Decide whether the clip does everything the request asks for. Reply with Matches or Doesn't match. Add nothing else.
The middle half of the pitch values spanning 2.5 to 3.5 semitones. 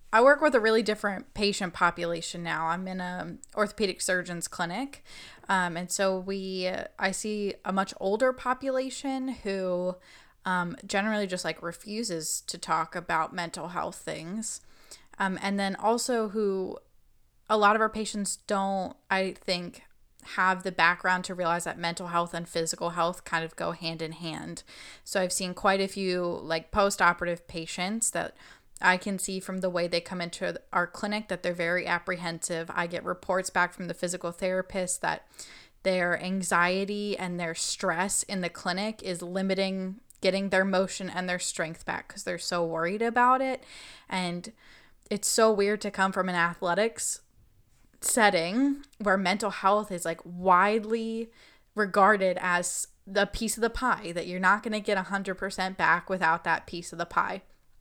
Matches